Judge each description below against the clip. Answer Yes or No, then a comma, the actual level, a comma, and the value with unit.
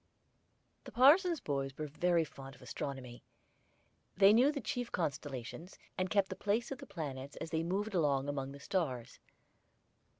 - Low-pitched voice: No, medium, 165 Hz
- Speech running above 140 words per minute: Yes, average, 160 wpm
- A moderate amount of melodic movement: No, wide, 6.8 semitones